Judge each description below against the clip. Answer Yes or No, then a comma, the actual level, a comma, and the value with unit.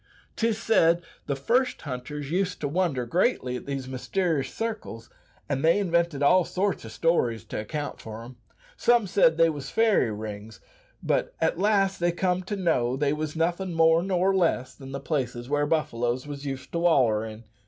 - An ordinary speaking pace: Yes, average, 175 wpm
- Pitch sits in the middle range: Yes, medium, 155 Hz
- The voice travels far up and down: Yes, wide, 5.9 semitones